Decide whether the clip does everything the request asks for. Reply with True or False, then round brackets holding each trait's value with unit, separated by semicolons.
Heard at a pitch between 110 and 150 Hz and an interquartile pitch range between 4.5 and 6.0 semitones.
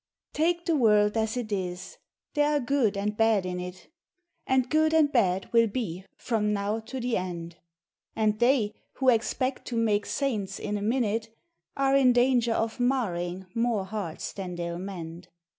False (220 Hz; 4.8 semitones)